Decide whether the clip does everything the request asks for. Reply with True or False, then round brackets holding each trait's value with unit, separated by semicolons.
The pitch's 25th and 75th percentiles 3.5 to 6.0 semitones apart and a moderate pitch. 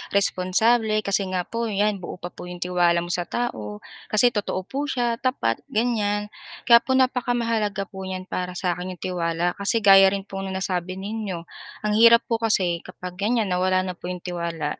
False (3.8 semitones; 195 Hz)